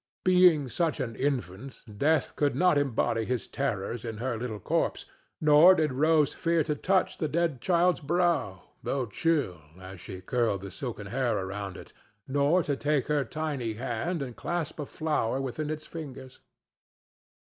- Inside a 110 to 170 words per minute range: Yes, average, 160 wpm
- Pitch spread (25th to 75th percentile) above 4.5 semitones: Yes, wide, 5.5 semitones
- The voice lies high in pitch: No, medium, 140 Hz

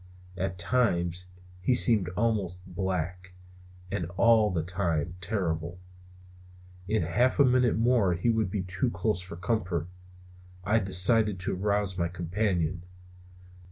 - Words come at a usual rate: No, slow, 130 wpm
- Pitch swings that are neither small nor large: Yes, average, 3.8 semitones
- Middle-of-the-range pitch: No, very low, 95 Hz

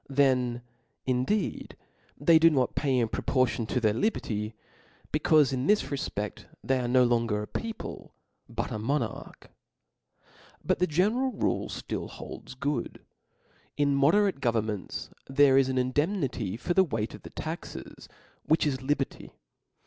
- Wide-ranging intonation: No, average, 4.2 semitones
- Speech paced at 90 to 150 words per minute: Yes, average, 145 wpm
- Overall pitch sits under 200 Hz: Yes, low, 135 Hz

